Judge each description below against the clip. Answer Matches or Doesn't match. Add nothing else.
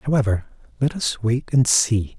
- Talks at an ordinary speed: Matches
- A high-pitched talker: Doesn't match